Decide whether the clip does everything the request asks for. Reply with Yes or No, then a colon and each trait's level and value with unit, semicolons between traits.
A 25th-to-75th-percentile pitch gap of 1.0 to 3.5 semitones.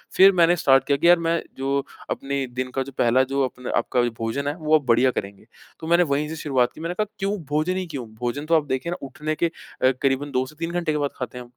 No: average, 4.1 semitones